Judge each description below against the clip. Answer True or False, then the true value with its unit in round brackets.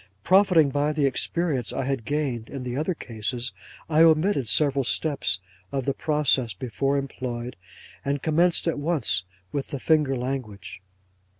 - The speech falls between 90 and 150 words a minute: True (145 wpm)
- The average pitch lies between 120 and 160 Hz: True (140 Hz)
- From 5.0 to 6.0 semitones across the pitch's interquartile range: False (3.6 semitones)